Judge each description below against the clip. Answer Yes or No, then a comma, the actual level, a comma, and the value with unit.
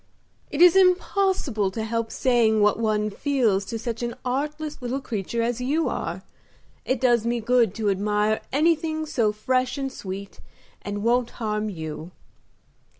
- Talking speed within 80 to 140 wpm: No, average, 150 wpm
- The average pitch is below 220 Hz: No, high, 235 Hz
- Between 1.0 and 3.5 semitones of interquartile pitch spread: No, average, 4.2 semitones